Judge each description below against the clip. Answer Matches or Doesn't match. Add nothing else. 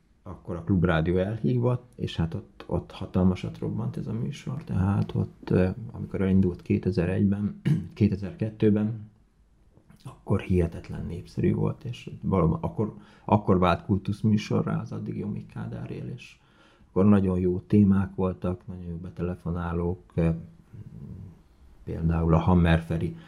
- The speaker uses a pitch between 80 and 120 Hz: Matches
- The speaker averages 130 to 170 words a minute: Doesn't match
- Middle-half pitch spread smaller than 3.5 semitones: Matches